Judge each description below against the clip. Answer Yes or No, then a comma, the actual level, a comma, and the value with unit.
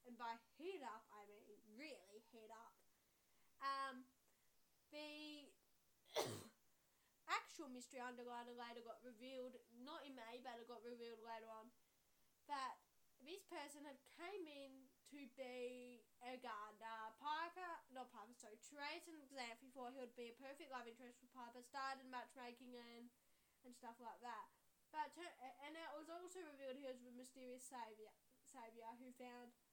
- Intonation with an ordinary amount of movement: Yes, average, 3.4 semitones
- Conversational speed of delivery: Yes, average, 150 wpm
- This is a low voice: No, very high, 250 Hz